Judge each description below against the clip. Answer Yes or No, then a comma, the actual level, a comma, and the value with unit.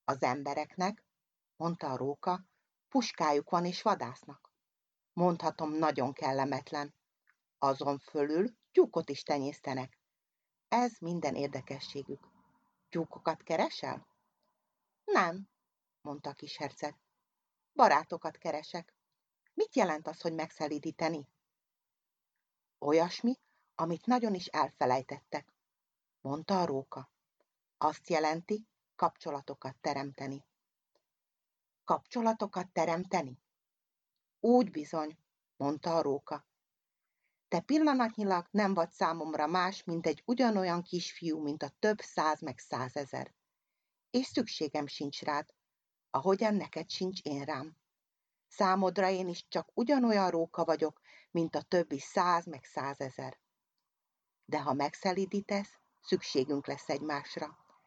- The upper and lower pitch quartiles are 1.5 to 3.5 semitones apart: No, average, 4.8 semitones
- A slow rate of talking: Yes, slow, 100 wpm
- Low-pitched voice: No, medium, 165 Hz